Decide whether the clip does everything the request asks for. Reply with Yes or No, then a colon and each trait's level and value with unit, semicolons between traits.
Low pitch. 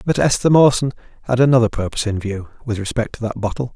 Yes: low, 120 Hz